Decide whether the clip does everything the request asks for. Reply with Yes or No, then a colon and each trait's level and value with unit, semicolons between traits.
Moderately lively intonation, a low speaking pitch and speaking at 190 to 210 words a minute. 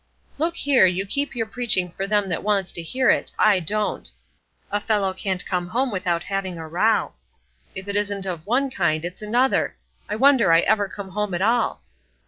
No: average, 3.7 semitones; high, 200 Hz; average, 195 wpm